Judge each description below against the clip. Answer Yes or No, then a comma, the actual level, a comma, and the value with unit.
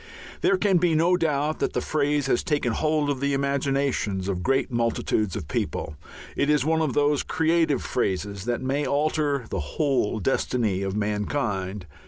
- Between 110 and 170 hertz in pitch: Yes, medium, 140 Hz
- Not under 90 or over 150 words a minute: No, average, 170 wpm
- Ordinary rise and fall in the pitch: No, wide, 6.0 semitones